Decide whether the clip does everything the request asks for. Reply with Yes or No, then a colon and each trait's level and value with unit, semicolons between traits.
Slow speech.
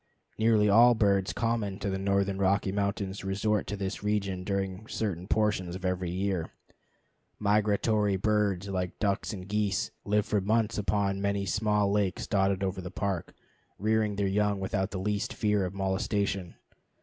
No: average, 160 wpm